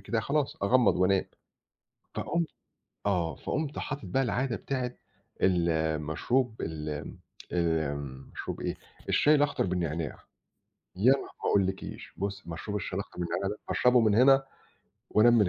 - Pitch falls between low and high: No, low, 100 Hz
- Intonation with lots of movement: Yes, wide, 6.9 semitones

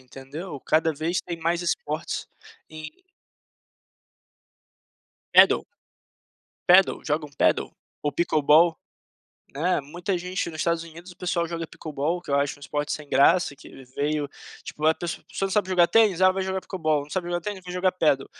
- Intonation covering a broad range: No, average, 3.2 semitones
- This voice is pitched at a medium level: Yes, medium, 165 Hz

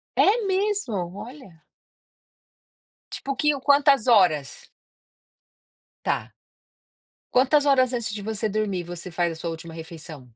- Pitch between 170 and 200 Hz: No, high, 215 Hz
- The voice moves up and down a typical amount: No, wide, 8.4 semitones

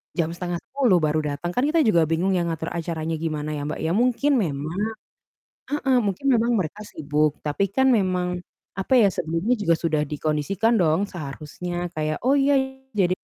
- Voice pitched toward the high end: No, medium, 175 Hz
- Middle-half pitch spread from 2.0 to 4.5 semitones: No, average, 5.1 semitones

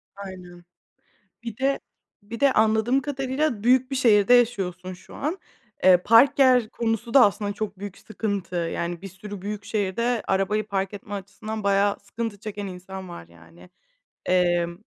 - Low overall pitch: No, high, 205 Hz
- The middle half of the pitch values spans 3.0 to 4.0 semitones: Yes, average, 3.7 semitones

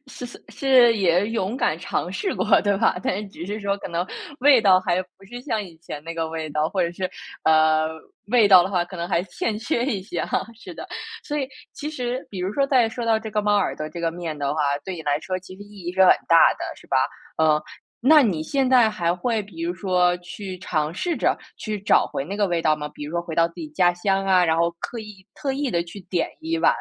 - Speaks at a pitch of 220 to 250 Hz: No, high, 190 Hz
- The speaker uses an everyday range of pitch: Yes, average, 4.9 semitones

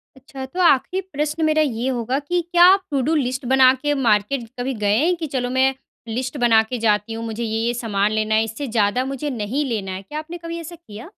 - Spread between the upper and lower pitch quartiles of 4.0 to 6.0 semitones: Yes, average, 4.9 semitones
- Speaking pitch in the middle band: No, very high, 255 Hz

